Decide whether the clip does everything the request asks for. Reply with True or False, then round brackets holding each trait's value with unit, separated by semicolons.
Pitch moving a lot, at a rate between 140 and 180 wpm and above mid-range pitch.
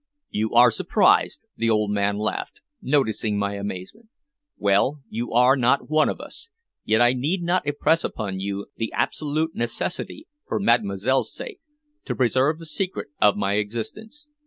False (6.8 semitones; 155 wpm; 120 Hz)